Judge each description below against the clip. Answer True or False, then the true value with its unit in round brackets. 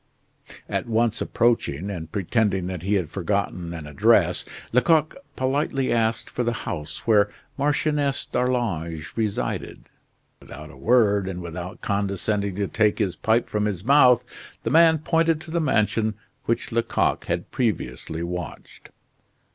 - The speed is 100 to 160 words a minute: True (140 wpm)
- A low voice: True (105 Hz)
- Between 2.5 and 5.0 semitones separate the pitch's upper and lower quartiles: False (5.6 semitones)